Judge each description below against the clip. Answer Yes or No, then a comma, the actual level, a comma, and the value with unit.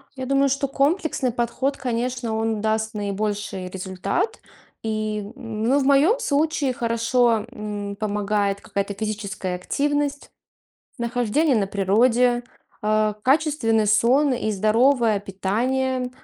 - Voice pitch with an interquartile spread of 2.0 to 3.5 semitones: No, average, 4.0 semitones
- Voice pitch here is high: Yes, high, 230 Hz